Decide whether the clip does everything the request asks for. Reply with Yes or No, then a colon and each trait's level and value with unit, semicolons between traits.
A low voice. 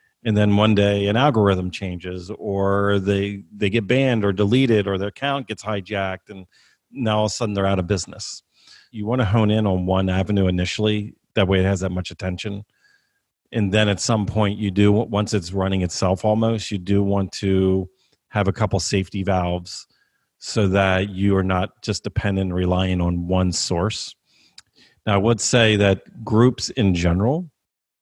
Yes: low, 100 Hz